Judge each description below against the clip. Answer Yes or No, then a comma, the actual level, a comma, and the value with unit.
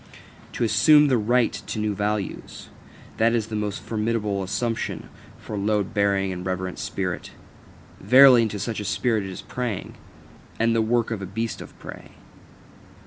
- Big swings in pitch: No, average, 2.7 semitones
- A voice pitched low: Yes, low, 105 Hz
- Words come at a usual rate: Yes, average, 165 wpm